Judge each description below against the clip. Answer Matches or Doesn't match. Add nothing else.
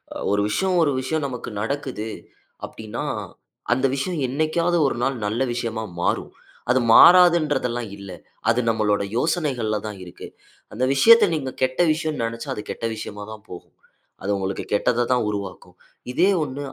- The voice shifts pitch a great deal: Matches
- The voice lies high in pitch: Doesn't match